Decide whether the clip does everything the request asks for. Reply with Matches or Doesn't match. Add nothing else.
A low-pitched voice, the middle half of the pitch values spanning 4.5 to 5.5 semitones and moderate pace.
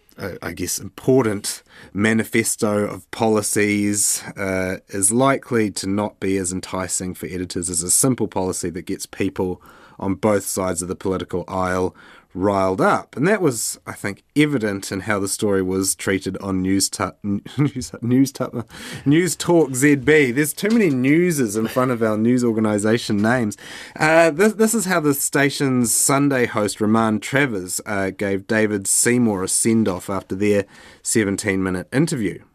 Matches